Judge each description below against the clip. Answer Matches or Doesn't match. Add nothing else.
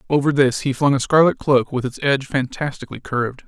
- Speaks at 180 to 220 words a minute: Matches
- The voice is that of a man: Matches